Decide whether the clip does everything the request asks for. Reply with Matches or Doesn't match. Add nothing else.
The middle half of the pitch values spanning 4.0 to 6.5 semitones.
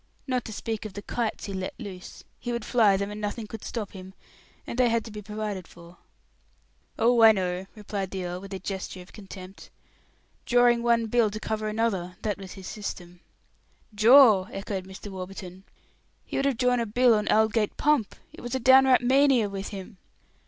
Doesn't match